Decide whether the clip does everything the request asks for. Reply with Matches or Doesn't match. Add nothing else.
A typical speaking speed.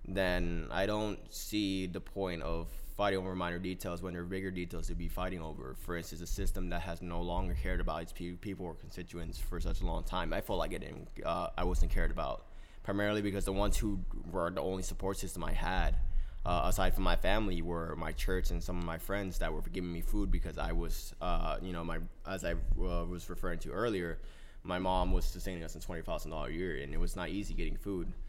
Doesn't match